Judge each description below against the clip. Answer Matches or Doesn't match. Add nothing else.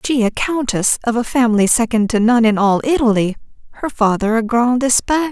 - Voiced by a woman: Matches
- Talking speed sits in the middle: Matches